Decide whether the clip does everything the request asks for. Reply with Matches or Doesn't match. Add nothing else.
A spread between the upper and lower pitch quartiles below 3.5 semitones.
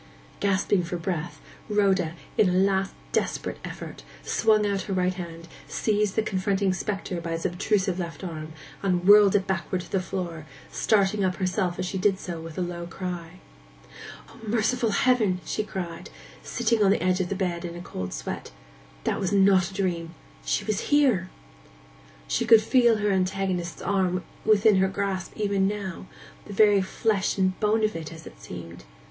Matches